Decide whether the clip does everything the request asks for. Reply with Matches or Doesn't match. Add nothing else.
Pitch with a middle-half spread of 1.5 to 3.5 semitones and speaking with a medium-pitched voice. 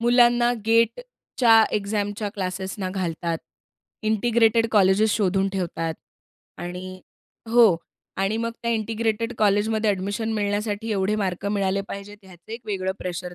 Doesn't match